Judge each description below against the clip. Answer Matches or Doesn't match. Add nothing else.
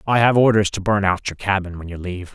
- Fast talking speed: Matches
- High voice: Doesn't match